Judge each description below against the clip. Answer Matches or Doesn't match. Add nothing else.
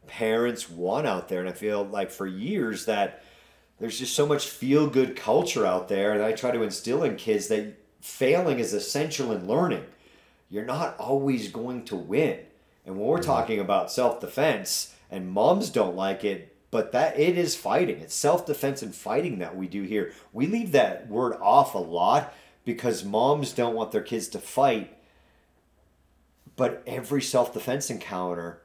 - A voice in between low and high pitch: Doesn't match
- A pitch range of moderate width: Doesn't match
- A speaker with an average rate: Matches